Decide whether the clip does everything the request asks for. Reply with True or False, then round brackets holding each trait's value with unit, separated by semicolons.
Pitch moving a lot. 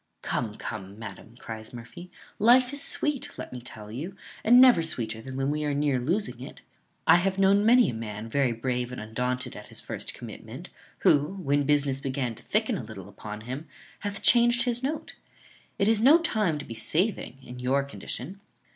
True (8.8 semitones)